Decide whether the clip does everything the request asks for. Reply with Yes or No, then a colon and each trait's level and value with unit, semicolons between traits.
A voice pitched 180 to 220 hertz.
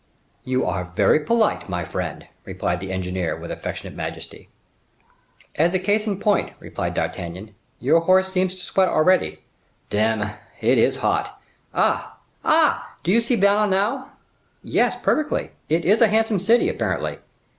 Yes: medium, 185 Hz